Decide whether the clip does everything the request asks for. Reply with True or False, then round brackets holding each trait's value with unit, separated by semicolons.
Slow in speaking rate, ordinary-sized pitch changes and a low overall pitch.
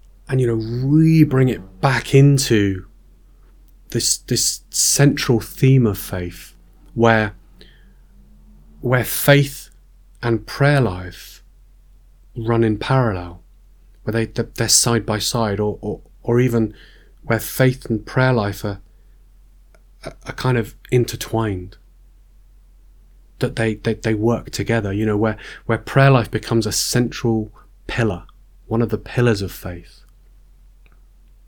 True (125 wpm; 3.3 semitones; 110 Hz)